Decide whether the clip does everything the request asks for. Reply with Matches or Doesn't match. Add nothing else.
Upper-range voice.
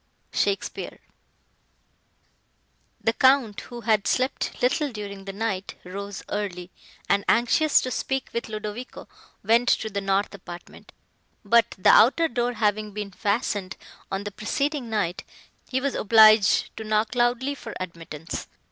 Matches